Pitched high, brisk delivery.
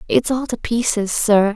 No: high, 220 Hz; average, 195 wpm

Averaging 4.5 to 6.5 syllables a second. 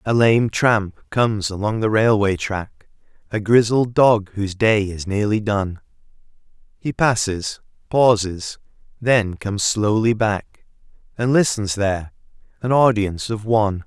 No: 4.2 syllables/s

